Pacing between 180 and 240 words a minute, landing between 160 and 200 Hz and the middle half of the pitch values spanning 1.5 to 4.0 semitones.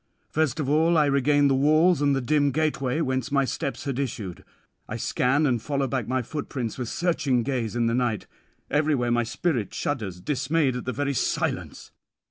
No: average, 185 wpm; low, 135 Hz; average, 3.2 semitones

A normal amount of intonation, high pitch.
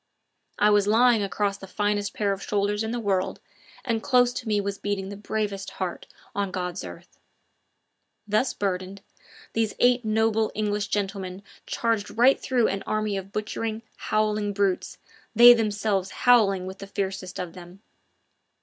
No: narrow, 2.1 semitones; high, 205 Hz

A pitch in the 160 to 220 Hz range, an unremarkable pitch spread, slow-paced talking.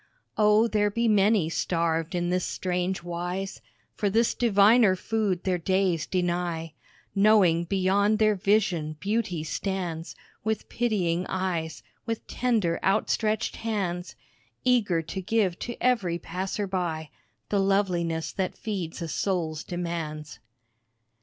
Yes: medium, 185 Hz; average, 3.5 semitones; slow, 120 wpm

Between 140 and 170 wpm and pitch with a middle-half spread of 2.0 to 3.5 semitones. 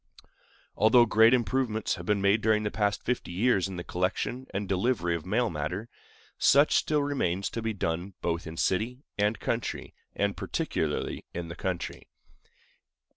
No: average, 160 wpm; average, 4.3 semitones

